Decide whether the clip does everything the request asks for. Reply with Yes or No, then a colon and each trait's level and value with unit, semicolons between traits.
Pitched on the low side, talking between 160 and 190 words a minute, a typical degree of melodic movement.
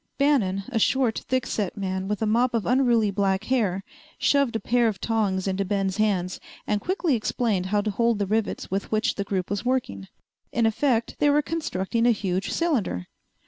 No: high, 215 Hz; average, 185 wpm; average, 4.0 semitones